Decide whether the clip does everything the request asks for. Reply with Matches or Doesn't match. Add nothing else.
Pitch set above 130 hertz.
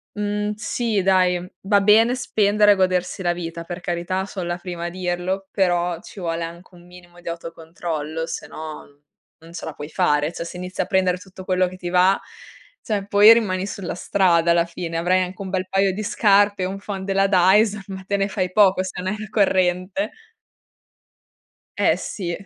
Matches